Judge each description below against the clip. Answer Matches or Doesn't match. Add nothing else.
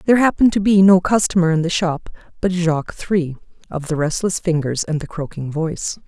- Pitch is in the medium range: Matches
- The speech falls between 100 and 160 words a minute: Doesn't match